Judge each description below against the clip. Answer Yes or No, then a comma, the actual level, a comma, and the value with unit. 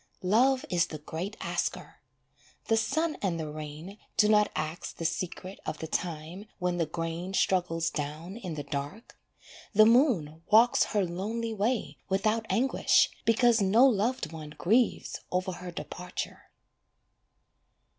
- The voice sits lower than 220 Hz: Yes, medium, 185 Hz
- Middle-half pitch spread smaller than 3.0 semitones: No, average, 5.2 semitones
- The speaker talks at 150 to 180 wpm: No, average, 140 wpm